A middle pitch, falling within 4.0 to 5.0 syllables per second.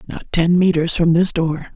Yes: medium, 170 Hz; 4.8 syllables/s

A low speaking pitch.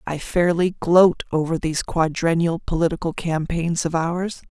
No: medium, 165 Hz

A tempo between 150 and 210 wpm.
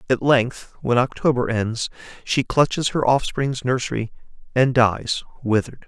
No: slow, 135 wpm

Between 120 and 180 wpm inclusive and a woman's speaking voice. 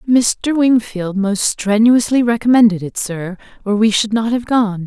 Yes: average, 160 wpm; female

